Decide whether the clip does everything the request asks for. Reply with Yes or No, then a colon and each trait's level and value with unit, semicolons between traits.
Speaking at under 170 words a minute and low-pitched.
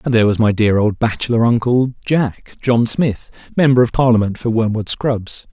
No: average, 175 wpm; low, 115 Hz